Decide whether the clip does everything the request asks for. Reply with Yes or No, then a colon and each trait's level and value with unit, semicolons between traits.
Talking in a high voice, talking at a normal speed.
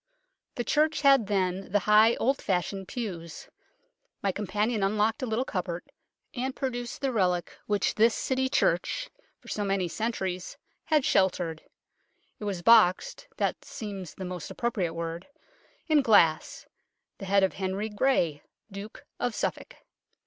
Yes: high, 205 Hz; average, 145 wpm